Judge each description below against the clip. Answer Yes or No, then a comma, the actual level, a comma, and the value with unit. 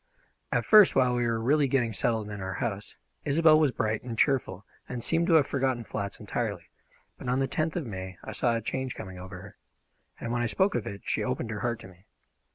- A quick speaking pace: Yes, fast, 230 wpm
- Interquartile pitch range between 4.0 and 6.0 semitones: Yes, average, 4.6 semitones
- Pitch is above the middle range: No, low, 120 Hz